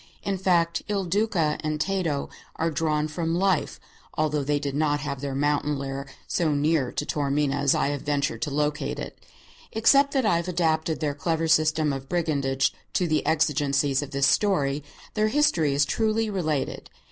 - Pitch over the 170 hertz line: No, medium, 155 Hz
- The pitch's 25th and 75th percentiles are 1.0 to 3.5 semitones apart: Yes, average, 3.2 semitones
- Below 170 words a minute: No, average, 175 wpm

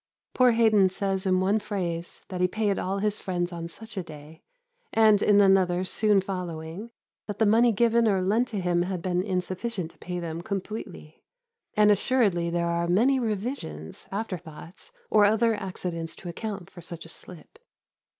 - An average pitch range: Yes, average, 3.6 semitones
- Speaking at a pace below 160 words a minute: No, average, 175 wpm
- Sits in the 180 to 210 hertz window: Yes, high, 190 Hz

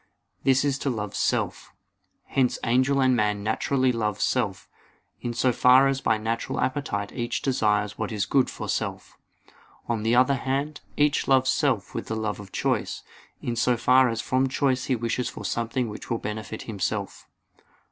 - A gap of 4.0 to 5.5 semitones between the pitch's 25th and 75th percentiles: No, average, 3.2 semitones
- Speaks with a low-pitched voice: Yes, low, 120 Hz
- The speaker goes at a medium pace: Yes, average, 175 wpm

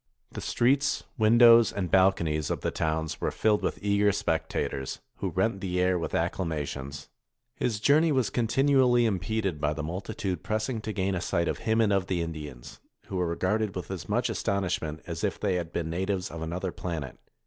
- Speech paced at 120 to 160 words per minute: No, average, 185 wpm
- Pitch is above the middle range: No, very low, 95 Hz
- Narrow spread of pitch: No, average, 4.7 semitones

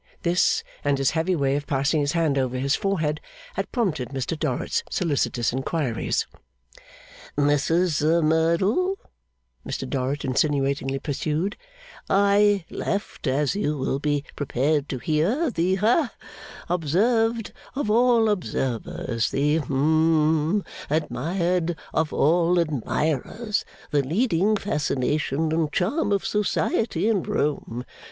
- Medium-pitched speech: Yes, medium, 160 Hz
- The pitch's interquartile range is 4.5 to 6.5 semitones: Yes, average, 5.3 semitones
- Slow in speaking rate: Yes, slow, 115 wpm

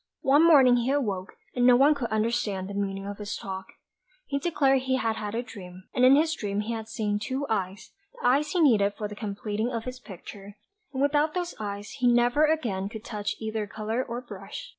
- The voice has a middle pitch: No, high, 225 Hz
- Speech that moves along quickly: Yes, fast, 215 wpm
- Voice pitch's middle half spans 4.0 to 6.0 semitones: Yes, average, 4.4 semitones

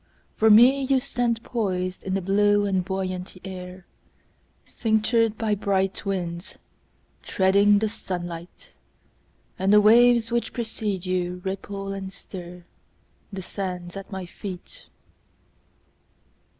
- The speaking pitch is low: No, high, 195 Hz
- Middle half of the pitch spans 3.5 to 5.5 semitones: No, average, 2.9 semitones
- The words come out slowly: Yes, slow, 90 wpm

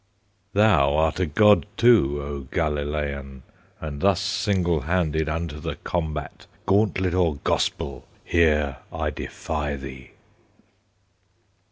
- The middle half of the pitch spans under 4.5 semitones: Yes, average, 4.0 semitones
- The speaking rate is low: Yes, slow, 110 wpm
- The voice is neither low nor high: No, very low, 80 Hz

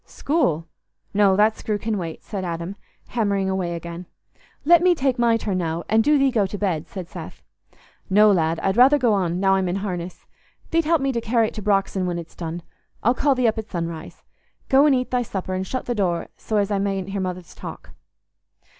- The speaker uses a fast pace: Yes, fast, 215 wpm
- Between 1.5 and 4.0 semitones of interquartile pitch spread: No, average, 4.7 semitones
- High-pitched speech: Yes, high, 200 Hz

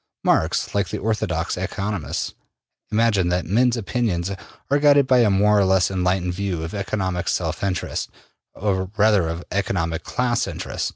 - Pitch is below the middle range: Yes, low, 100 Hz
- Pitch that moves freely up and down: No, average, 3.4 semitones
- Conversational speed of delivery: Yes, average, 155 wpm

